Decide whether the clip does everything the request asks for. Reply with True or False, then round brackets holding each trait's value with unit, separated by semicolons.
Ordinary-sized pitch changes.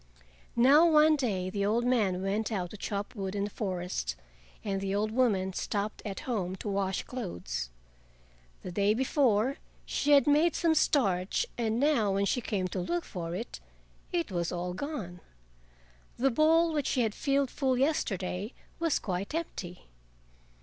False (6.3 semitones)